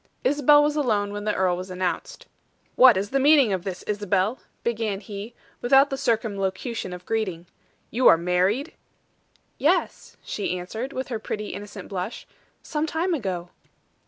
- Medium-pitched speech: No, high, 210 Hz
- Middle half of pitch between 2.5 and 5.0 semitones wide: No, wide, 5.5 semitones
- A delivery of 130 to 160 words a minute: Yes, average, 155 wpm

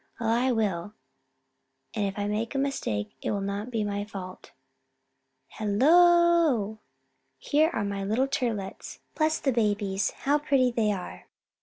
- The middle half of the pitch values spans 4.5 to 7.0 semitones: Yes, average, 5.1 semitones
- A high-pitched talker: Yes, high, 220 Hz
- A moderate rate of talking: Yes, average, 150 wpm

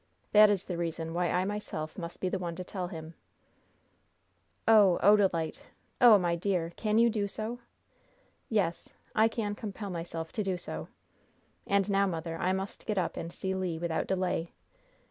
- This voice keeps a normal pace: Yes, average, 170 wpm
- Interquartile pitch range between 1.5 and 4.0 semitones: Yes, average, 3.3 semitones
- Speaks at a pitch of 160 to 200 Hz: Yes, medium, 185 Hz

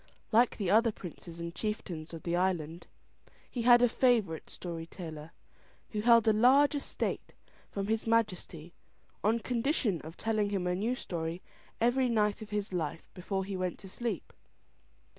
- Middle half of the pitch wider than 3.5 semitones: Yes, average, 4.9 semitones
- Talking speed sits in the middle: Yes, average, 160 wpm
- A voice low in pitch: No, high, 205 Hz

